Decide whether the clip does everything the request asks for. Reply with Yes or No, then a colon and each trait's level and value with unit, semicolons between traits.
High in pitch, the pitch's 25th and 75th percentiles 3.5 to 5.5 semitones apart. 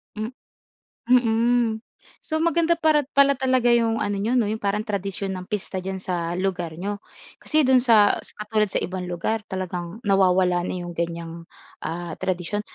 Yes: high, 205 Hz; average, 4.7 semitones